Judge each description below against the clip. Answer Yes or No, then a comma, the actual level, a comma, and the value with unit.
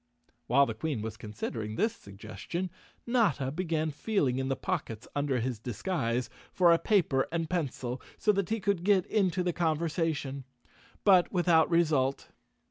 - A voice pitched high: No, medium, 160 Hz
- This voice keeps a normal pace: Yes, average, 150 wpm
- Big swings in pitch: Yes, wide, 5.9 semitones